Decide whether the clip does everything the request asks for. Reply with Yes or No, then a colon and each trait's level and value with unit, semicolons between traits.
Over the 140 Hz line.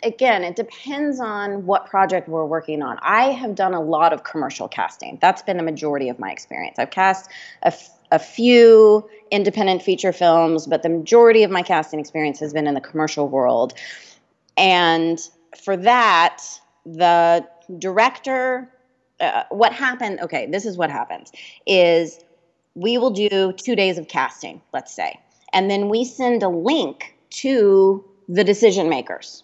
Yes: high, 190 Hz